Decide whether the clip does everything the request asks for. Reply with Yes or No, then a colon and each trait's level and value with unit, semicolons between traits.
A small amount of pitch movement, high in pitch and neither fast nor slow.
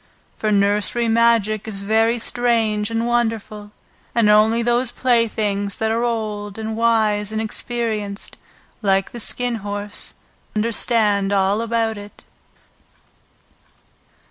No: narrow, 2.0 semitones; high, 220 Hz; slow, 115 wpm